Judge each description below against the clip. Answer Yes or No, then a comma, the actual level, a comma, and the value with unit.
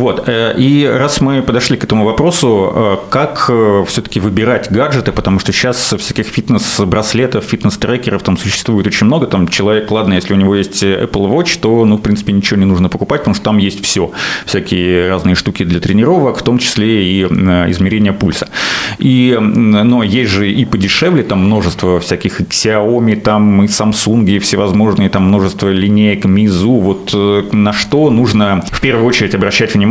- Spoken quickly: Yes, fast, 170 wpm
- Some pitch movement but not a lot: Yes, average, 3.0 semitones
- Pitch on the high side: No, low, 105 Hz